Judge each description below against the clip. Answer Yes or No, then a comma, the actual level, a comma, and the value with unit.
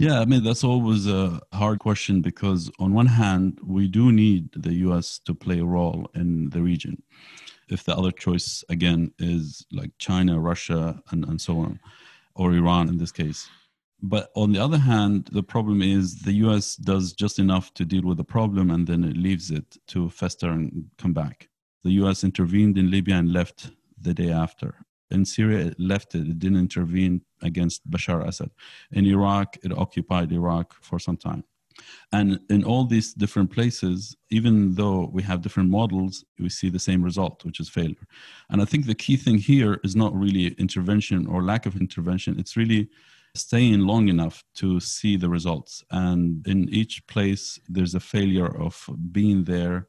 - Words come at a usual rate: Yes, average, 185 wpm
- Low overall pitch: Yes, very low, 95 Hz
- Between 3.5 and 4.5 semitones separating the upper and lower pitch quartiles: No, average, 2.8 semitones